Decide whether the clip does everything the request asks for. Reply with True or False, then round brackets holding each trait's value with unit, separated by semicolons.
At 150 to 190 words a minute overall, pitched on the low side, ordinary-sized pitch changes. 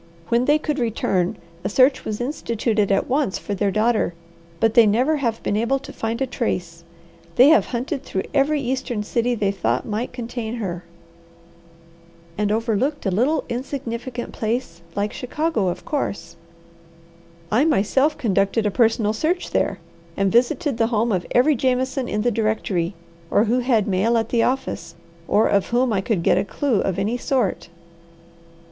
False (165 wpm; 230 Hz; 4.0 semitones)